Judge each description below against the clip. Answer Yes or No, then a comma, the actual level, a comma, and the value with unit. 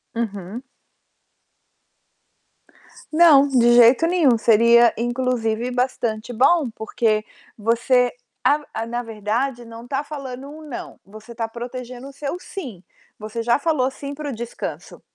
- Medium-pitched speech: No, high, 240 Hz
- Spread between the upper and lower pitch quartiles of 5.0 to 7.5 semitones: No, average, 3.1 semitones